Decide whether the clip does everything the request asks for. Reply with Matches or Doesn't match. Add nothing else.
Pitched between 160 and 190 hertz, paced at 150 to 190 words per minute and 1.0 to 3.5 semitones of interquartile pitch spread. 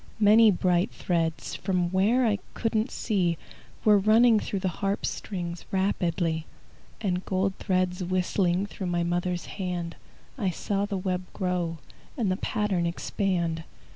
Doesn't match